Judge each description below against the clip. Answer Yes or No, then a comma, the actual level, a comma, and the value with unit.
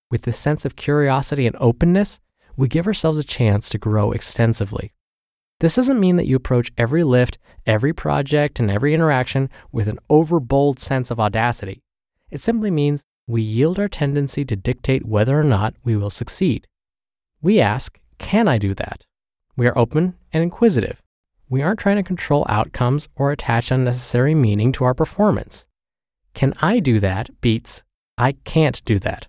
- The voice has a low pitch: Yes, low, 130 Hz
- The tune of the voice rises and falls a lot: No, average, 4.7 semitones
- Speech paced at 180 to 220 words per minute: No, average, 170 wpm